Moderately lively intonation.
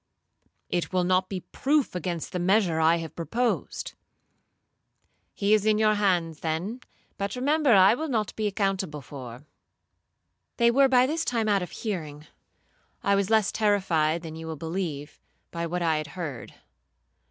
Yes: average, 5.0 semitones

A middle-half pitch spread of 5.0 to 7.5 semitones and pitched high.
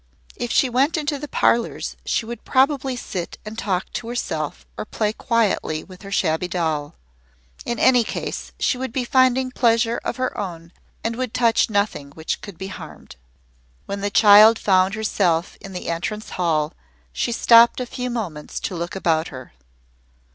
Yes: average, 5.3 semitones; high, 215 Hz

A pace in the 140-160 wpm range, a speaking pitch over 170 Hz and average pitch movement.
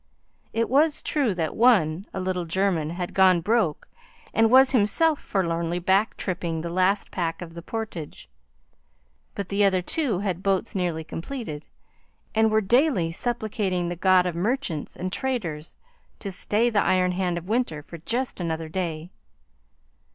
Yes: average, 155 wpm; medium, 185 Hz; average, 4.6 semitones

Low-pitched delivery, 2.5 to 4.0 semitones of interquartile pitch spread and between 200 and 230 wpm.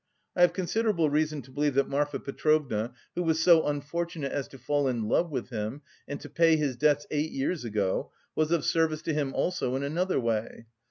No: medium, 145 Hz; average, 3.3 semitones; fast, 205 wpm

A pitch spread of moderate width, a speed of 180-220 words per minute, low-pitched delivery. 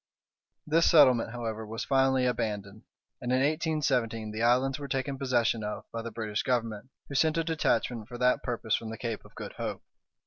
Yes: average, 3.2 semitones; average, 185 wpm; low, 120 Hz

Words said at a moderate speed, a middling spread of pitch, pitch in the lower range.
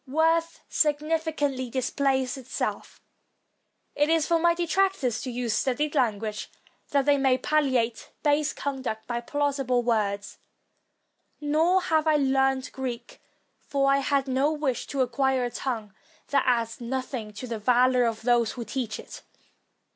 No: average, 145 wpm; average, 3.3 semitones; very high, 265 Hz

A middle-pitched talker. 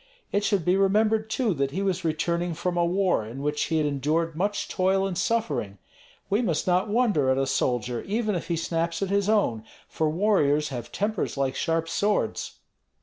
Yes: medium, 175 Hz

